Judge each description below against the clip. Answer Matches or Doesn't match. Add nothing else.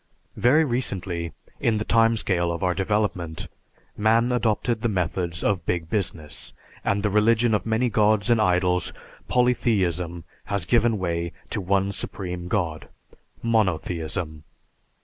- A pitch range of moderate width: Matches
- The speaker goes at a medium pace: Doesn't match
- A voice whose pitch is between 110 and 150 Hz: Doesn't match